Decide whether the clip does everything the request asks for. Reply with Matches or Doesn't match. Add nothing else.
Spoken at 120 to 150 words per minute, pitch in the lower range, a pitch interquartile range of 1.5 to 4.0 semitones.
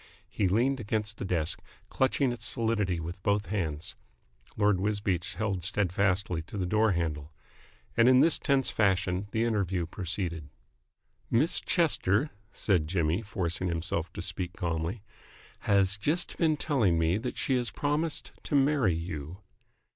Doesn't match